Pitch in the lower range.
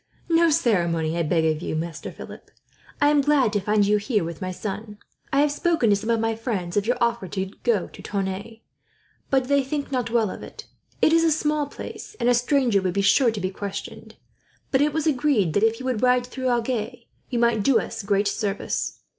No: high, 225 Hz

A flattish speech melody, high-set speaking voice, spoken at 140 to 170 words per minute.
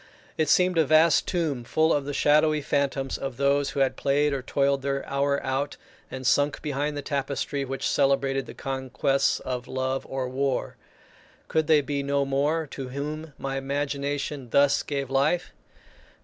No: narrow, 1.3 semitones; medium, 140 Hz; average, 165 wpm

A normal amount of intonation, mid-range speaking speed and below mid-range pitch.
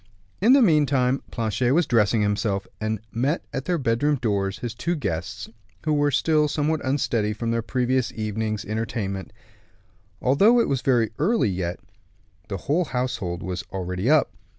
No: wide, 5.7 semitones; average, 155 wpm; low, 120 Hz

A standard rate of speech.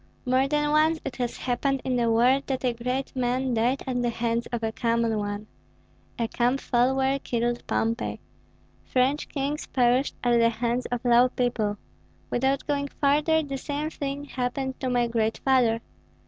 Yes: average, 170 wpm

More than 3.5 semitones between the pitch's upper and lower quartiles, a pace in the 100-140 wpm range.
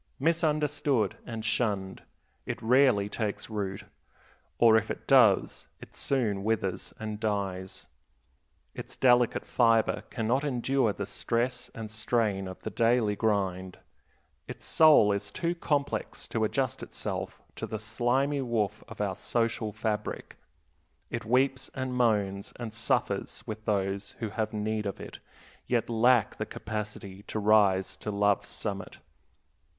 No: average, 3.2 semitones; slow, 135 wpm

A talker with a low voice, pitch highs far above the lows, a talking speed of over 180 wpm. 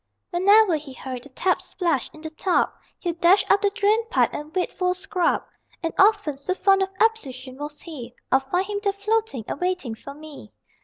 No: very high, 355 Hz; wide, 5.8 semitones; fast, 205 wpm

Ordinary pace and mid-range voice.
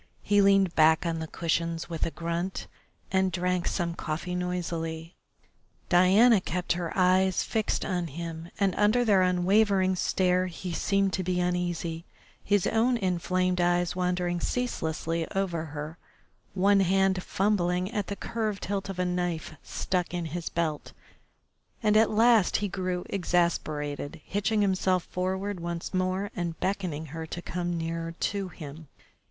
Yes: average, 145 wpm; medium, 180 Hz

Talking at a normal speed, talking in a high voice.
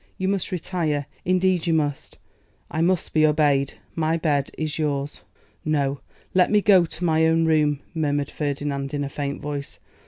No: average, 165 wpm; medium, 155 Hz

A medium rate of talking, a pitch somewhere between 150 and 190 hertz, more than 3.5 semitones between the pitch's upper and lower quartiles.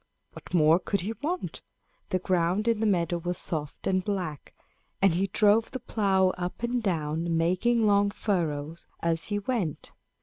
Yes: average, 165 wpm; medium, 185 Hz; average, 3.9 semitones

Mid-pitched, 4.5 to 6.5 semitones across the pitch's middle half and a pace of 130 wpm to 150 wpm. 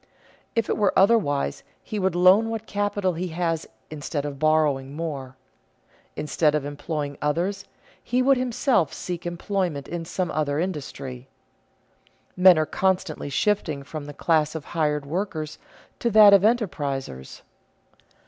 Yes: medium, 165 Hz; average, 5.1 semitones; average, 140 wpm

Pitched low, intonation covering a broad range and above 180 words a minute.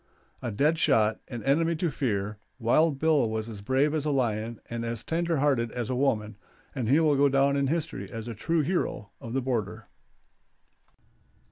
No: low, 130 Hz; average, 4.8 semitones; average, 190 wpm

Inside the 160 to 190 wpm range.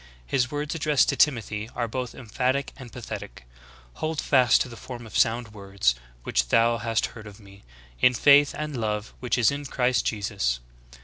Yes: average, 175 wpm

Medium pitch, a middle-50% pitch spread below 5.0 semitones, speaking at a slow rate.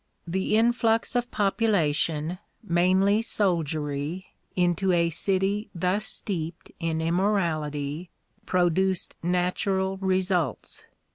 Yes: medium, 180 Hz; average, 2.9 semitones; slow, 85 wpm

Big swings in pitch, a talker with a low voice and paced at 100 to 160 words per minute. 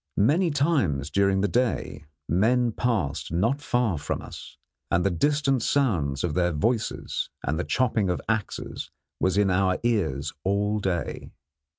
Yes: wide, 5.9 semitones; low, 100 Hz; average, 150 wpm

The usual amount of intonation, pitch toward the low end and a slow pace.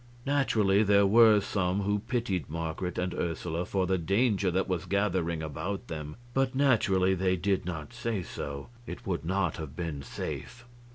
No: average, 3.3 semitones; very low, 95 Hz; average, 165 wpm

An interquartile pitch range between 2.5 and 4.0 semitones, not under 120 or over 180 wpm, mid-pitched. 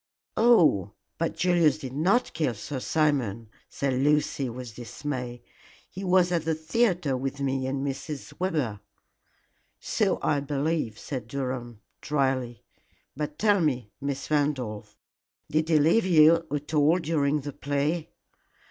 Yes: average, 3.6 semitones; slow, 135 wpm; medium, 145 Hz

